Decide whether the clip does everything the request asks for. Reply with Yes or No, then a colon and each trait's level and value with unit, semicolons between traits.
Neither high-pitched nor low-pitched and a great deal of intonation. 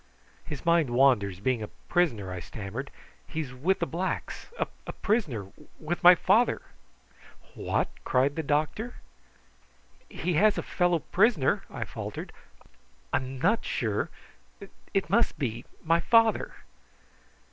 Yes: medium, 155 Hz; wide, 6.2 semitones